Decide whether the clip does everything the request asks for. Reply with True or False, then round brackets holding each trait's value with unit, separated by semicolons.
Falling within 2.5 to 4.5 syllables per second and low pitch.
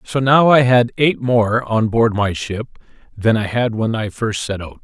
True (4.4 syllables/s; 115 Hz)